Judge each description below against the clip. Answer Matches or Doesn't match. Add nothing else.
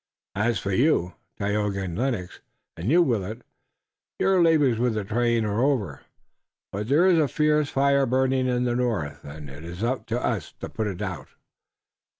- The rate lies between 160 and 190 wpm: Matches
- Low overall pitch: Matches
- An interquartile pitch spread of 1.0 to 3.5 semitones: Doesn't match